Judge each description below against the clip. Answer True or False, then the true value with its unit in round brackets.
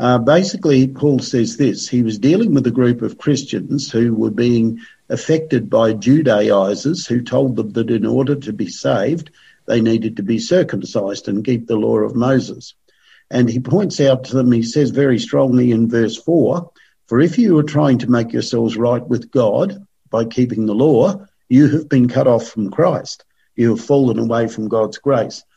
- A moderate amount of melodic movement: True (3.8 semitones)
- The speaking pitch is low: True (125 Hz)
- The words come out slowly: False (190 wpm)